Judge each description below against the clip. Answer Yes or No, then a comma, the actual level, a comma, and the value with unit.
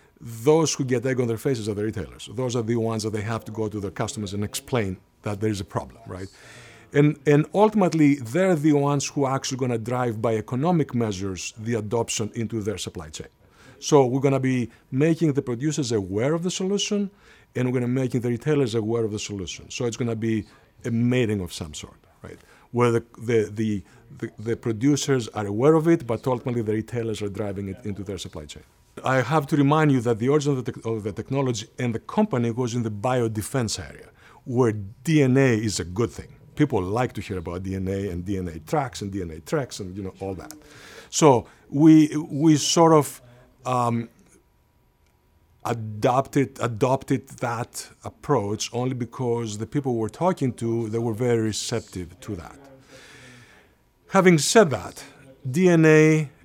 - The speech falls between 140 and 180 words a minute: No, average, 190 wpm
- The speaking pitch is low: Yes, low, 120 Hz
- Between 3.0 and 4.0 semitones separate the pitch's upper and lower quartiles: No, average, 4.4 semitones